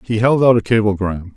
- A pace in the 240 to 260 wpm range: No, fast, 220 wpm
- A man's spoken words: Yes, male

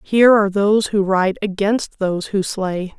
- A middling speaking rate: Yes, average, 180 wpm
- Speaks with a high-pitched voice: Yes, high, 200 Hz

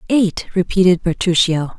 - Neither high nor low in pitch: Yes, medium, 180 Hz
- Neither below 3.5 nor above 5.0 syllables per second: Yes, 4.6 syllables/s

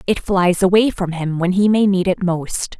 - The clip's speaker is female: Yes, female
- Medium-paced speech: No, fast, 235 wpm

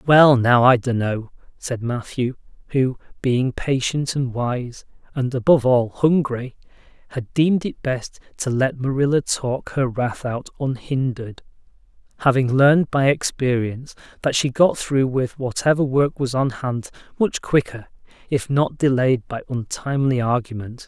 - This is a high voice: No, low, 130 Hz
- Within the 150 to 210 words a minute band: No, average, 140 wpm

